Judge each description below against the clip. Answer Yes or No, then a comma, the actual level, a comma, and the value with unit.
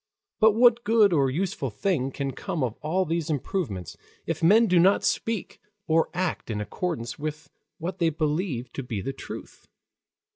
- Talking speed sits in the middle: Yes, average, 170 wpm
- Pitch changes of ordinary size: No, wide, 5.7 semitones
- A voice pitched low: No, medium, 160 Hz